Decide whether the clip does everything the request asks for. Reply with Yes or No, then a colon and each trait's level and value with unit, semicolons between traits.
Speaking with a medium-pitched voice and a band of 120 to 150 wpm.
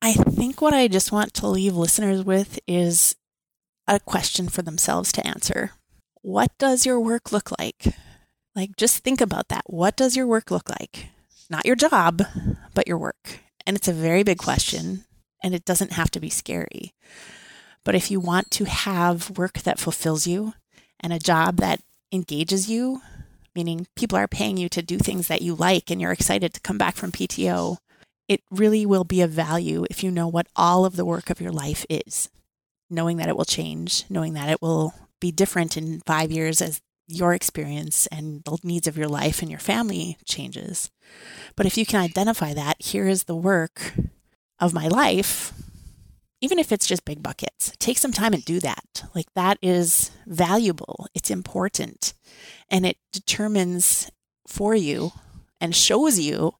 No: medium, 180 Hz; average, 180 wpm